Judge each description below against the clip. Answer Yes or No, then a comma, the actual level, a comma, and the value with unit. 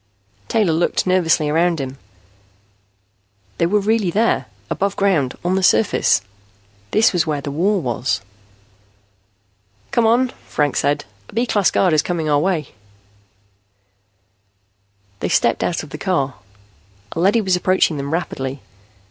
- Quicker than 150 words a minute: No, average, 140 wpm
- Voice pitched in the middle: Yes, medium, 175 Hz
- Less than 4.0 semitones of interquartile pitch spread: No, average, 5.0 semitones